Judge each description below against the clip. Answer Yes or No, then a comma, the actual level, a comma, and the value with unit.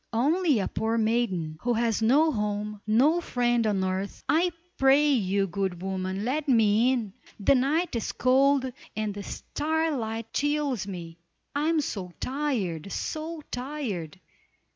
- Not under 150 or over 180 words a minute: No, average, 140 wpm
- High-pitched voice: Yes, high, 230 Hz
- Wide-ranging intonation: Yes, wide, 6.2 semitones